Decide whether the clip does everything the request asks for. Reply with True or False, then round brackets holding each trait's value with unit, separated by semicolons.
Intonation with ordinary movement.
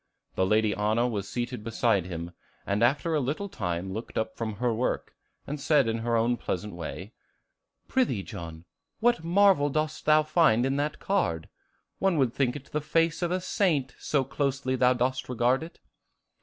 False (5.8 semitones)